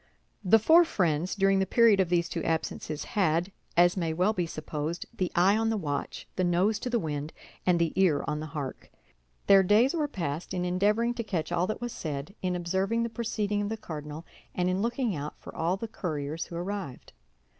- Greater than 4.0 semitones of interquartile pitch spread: Yes, average, 4.5 semitones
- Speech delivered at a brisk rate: Yes, fast, 210 wpm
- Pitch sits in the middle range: Yes, medium, 180 Hz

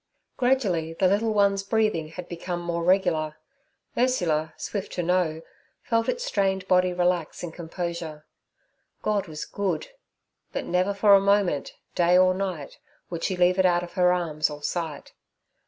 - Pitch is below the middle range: No, medium, 180 Hz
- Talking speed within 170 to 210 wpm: No, average, 155 wpm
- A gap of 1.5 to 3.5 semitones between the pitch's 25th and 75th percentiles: Yes, average, 2.9 semitones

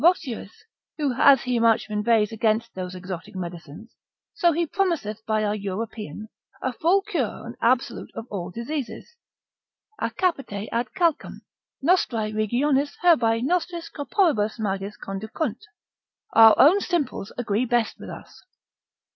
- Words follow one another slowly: Yes, slow, 130 wpm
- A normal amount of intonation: No, wide, 6.1 semitones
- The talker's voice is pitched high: Yes, high, 230 Hz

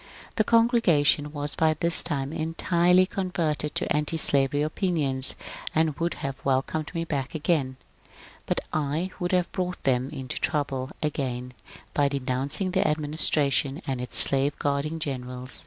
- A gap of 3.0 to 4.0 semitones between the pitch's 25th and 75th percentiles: Yes, average, 3.5 semitones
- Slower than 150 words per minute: Yes, average, 140 wpm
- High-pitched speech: No, medium, 150 Hz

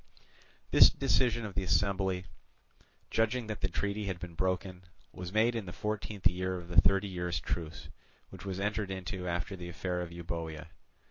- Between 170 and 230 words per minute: Yes, average, 175 wpm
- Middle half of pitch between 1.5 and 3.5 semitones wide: Yes, narrow, 2.6 semitones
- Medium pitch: No, very low, 95 Hz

